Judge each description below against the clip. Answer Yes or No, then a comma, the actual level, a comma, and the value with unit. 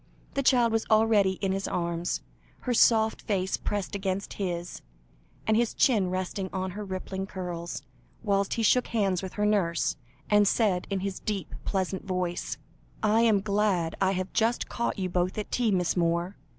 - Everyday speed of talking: Yes, average, 175 wpm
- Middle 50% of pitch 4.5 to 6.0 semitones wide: No, average, 2.7 semitones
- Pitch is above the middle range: Yes, high, 195 Hz